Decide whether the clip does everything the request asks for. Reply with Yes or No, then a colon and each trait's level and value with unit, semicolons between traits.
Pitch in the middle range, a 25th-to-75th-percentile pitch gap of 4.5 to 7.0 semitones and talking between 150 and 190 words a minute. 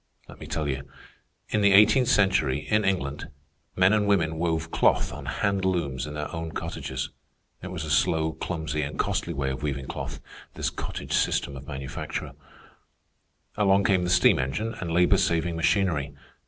No: very low, 80 Hz; average, 4.8 semitones; average, 170 wpm